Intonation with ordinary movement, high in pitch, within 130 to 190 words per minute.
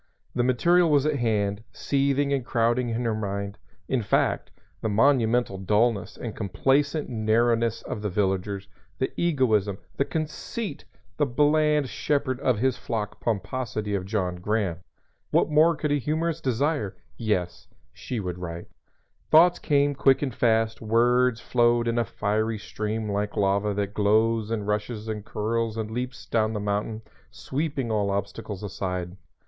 No: average, 4.2 semitones; low, 115 Hz; average, 150 wpm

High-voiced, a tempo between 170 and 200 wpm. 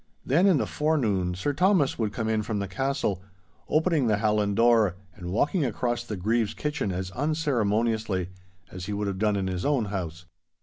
No: low, 110 Hz; average, 185 wpm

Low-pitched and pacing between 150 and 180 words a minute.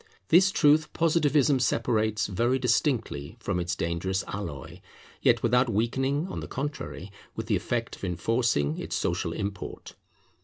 No: low, 115 Hz; average, 140 wpm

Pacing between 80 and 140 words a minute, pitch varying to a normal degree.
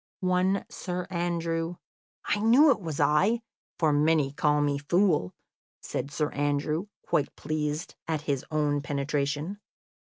Yes: slow, 135 wpm; average, 3.4 semitones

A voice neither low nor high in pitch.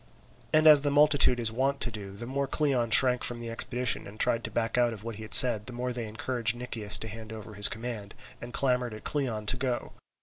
No: low, 120 Hz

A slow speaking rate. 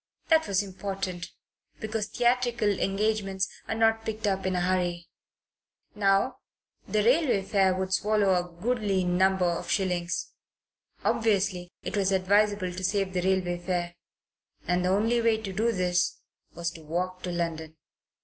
No: average, 150 wpm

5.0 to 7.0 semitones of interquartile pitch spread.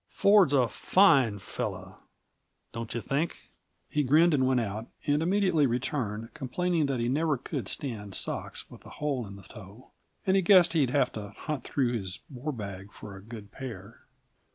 Yes: wide, 5.6 semitones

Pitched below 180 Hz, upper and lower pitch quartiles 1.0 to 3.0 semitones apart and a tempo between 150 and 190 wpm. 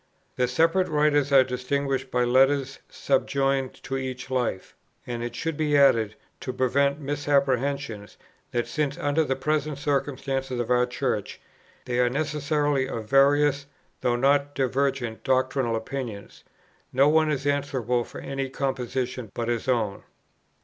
No: low, 135 Hz; narrow, 2.4 semitones; average, 140 wpm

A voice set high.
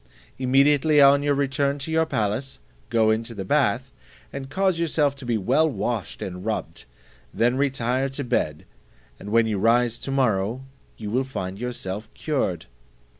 No: low, 125 Hz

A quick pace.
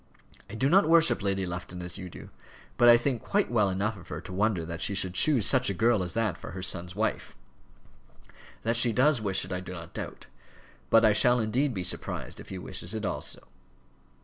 Yes: fast, 220 wpm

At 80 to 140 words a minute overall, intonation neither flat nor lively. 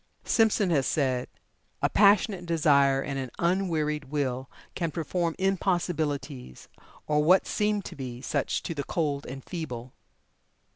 Yes: slow, 135 wpm; average, 4.7 semitones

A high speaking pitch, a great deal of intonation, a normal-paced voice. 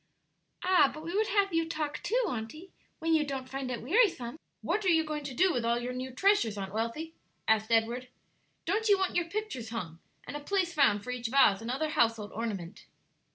No: very high, 275 Hz; wide, 6.9 semitones; fast, 210 wpm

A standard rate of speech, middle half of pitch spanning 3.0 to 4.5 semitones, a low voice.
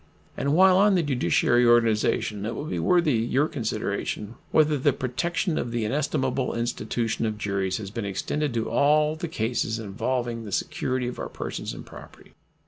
No: average, 170 wpm; average, 5.2 semitones; low, 125 Hz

